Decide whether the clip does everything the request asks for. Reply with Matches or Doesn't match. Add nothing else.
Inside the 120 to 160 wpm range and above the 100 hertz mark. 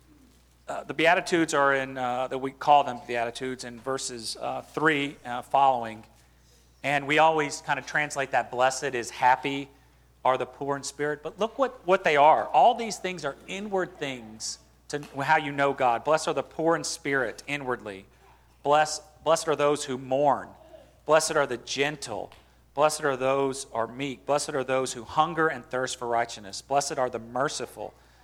Doesn't match